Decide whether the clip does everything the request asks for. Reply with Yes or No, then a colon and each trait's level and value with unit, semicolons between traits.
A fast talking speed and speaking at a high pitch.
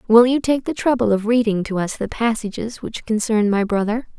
Yes: fast, 215 wpm; high, 225 Hz